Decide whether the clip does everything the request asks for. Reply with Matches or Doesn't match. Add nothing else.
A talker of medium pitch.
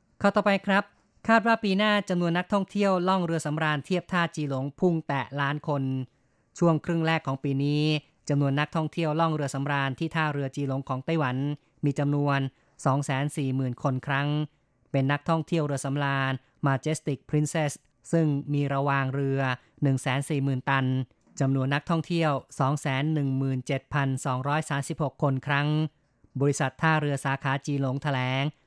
Matches